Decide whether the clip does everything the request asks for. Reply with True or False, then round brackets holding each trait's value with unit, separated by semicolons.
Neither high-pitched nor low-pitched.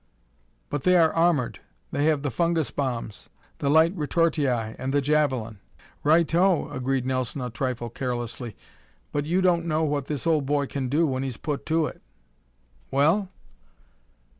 True (145 Hz)